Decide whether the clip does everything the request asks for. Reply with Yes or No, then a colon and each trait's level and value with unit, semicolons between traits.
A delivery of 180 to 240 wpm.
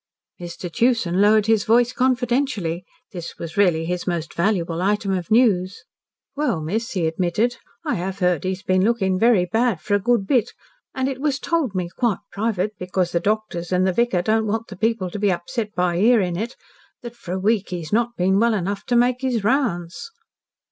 Yes: average, 195 wpm